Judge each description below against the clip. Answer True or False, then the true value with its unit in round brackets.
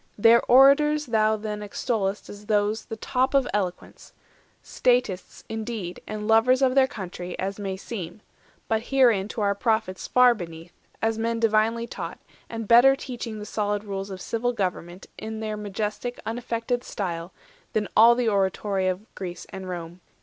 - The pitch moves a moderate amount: True (3.3 semitones)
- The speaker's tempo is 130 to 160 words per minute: True (155 wpm)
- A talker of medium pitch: False (215 Hz)